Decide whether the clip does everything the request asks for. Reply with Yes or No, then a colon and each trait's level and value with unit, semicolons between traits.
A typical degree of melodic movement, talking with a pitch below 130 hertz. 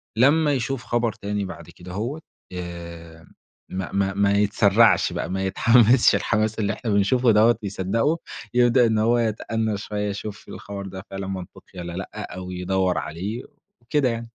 Yes: average, 3.6 semitones; low, 105 Hz